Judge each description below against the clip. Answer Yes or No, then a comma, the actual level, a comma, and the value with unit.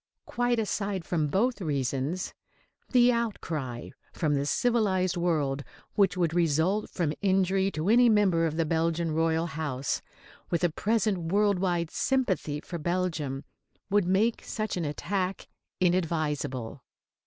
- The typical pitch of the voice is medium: Yes, medium, 175 Hz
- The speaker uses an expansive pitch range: No, average, 4.3 semitones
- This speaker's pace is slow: Yes, slow, 130 wpm